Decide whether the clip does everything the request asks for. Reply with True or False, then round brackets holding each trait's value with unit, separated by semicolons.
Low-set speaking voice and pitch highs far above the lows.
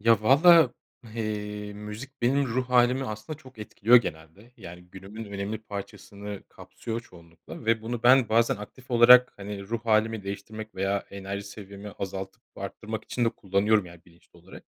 False (105 Hz; 3.0 semitones)